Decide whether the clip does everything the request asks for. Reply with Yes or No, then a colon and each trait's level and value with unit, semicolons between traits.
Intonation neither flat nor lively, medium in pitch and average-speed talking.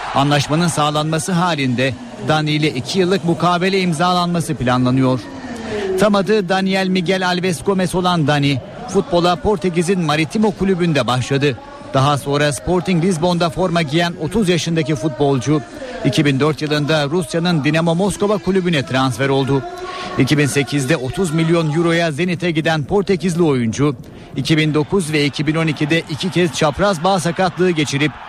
Yes: average, 3.9 semitones; medium, 165 Hz; average, 120 wpm